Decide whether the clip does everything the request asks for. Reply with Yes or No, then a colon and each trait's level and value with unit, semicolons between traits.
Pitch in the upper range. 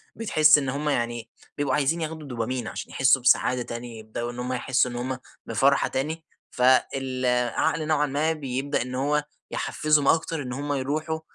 No: low, 135 Hz